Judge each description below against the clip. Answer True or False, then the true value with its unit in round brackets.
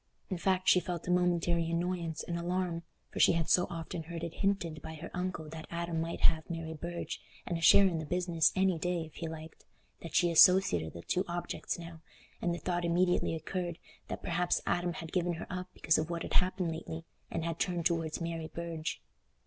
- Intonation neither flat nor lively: False (1.5 semitones)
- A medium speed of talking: False (210 wpm)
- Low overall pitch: False (170 Hz)